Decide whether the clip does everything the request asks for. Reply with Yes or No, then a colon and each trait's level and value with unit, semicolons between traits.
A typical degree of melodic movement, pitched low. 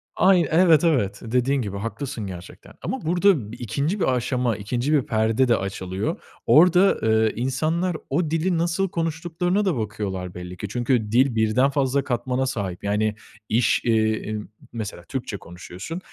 No: wide, 7.0 semitones; low, 125 Hz